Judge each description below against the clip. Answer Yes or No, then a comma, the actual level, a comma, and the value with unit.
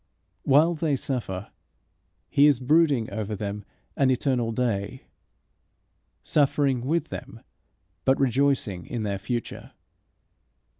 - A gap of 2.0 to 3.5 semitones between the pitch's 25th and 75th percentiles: No, average, 4.3 semitones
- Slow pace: Yes, slow, 105 wpm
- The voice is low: Yes, low, 130 Hz